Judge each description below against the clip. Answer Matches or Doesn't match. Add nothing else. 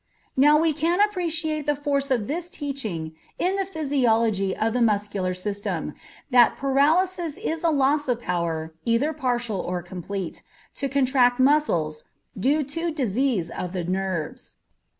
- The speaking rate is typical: Matches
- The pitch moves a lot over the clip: Matches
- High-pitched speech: Matches